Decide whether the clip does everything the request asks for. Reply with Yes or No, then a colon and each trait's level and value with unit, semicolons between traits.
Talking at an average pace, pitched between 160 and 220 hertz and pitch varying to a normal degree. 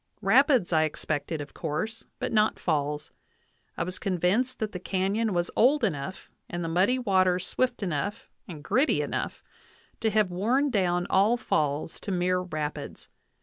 Yes: average, 155 wpm; medium, 185 Hz; average, 4.7 semitones